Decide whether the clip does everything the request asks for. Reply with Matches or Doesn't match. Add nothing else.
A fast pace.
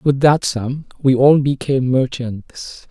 Doesn't match